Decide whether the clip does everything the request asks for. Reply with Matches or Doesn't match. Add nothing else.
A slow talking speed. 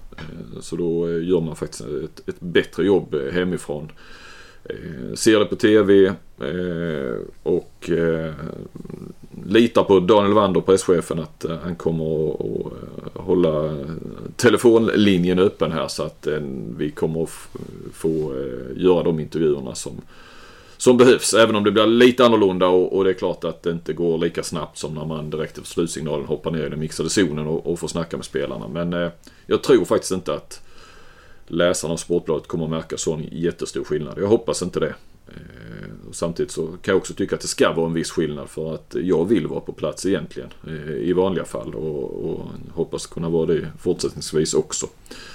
Doesn't match